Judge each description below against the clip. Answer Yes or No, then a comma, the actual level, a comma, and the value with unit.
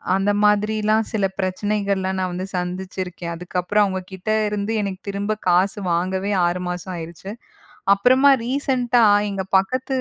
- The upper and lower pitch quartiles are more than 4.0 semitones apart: No, narrow, 2.4 semitones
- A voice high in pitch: Yes, high, 195 Hz